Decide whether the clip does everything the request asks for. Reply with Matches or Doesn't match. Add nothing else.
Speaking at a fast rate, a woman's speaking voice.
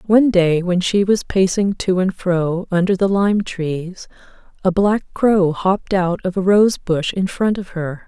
Doesn't match